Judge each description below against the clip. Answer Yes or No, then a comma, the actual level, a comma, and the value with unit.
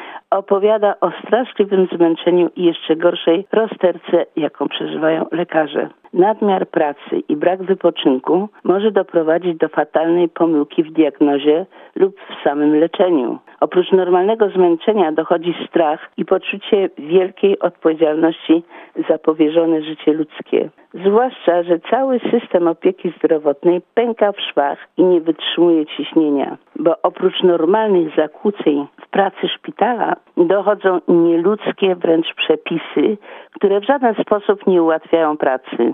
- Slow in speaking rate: Yes, slow, 120 wpm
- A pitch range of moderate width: Yes, average, 3.7 semitones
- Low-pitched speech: No, medium, 175 Hz